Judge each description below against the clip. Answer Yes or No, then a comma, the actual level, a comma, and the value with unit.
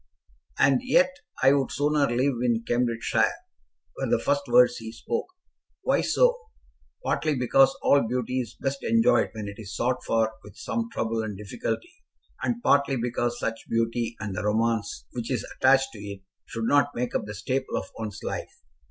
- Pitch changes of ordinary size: Yes, average, 3.7 semitones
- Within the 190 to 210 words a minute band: No, average, 175 wpm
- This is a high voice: No, low, 120 Hz